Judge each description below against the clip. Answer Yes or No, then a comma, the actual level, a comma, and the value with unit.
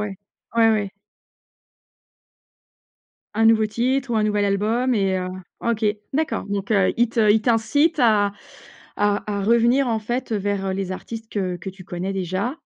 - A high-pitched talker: Yes, high, 215 Hz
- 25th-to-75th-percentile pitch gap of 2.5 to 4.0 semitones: Yes, average, 2.9 semitones